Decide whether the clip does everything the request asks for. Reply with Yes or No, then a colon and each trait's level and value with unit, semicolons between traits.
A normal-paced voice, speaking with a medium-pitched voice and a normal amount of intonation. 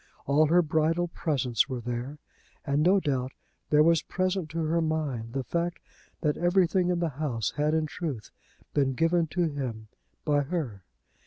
Yes: average, 165 wpm; medium, 155 Hz; average, 3.9 semitones